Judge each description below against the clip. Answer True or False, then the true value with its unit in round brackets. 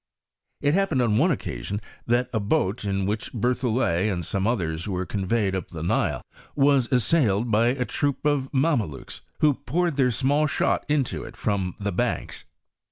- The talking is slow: False (170 wpm)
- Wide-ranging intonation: True (6.0 semitones)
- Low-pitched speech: True (120 Hz)